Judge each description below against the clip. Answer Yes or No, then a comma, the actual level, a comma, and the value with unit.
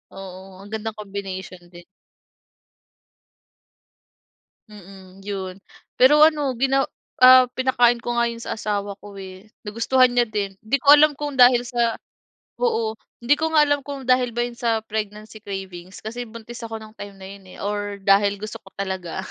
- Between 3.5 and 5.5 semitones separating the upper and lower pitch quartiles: Yes, average, 4.0 semitones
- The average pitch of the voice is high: Yes, high, 220 Hz